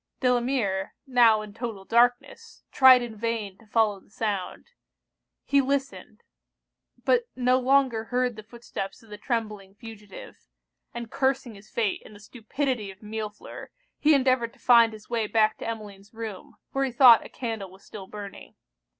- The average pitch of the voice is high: Yes, high, 225 Hz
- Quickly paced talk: No, average, 160 wpm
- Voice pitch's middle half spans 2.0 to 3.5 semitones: Yes, average, 3.1 semitones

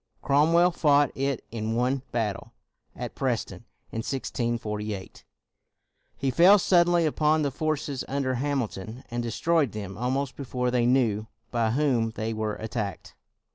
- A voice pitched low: Yes, low, 125 Hz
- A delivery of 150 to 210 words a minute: No, average, 140 wpm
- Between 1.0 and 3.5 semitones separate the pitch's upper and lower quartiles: No, average, 4.3 semitones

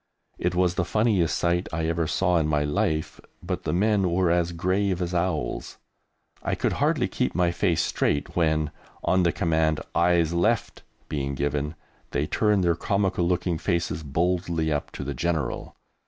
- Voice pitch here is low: Yes, very low, 85 Hz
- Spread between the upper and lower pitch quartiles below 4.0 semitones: Yes, narrow, 2.4 semitones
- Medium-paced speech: Yes, average, 170 wpm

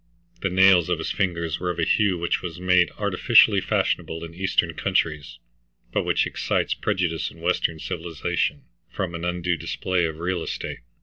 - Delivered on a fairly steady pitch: Yes, narrow, 1.8 semitones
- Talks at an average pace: Yes, average, 170 wpm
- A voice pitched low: Yes, very low, 85 Hz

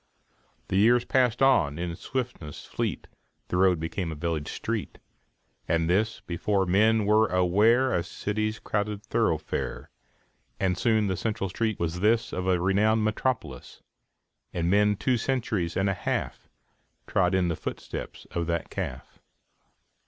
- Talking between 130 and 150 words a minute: Yes, average, 145 wpm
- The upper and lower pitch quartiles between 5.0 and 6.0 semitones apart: No, average, 4.0 semitones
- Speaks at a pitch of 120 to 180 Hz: No, low, 100 Hz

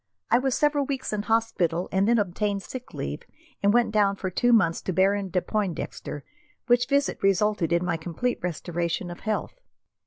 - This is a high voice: Yes, high, 200 Hz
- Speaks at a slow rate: No, average, 180 wpm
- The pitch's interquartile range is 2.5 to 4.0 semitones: No, average, 4.9 semitones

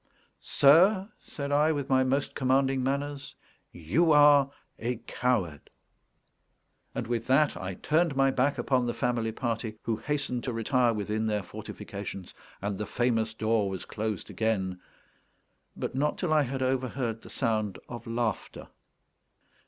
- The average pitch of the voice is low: Yes, low, 125 Hz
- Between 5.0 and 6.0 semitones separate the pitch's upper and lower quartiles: No, average, 3.9 semitones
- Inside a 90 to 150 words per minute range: Yes, average, 145 wpm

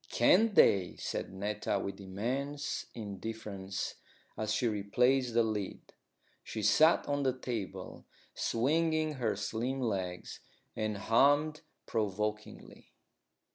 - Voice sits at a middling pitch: No, low, 110 Hz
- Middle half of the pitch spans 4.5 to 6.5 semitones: Yes, average, 4.8 semitones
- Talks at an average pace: No, slow, 105 wpm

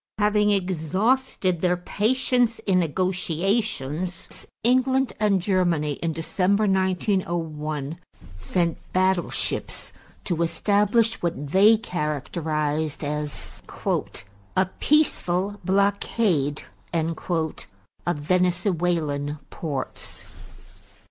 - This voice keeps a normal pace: No, slow, 75 wpm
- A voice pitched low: No, medium, 180 Hz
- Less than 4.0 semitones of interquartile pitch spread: No, average, 4.4 semitones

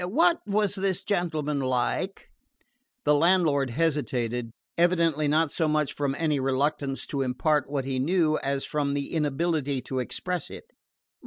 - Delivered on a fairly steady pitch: No, average, 3.8 semitones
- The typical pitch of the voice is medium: Yes, medium, 150 Hz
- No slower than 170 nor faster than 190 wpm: No, average, 145 wpm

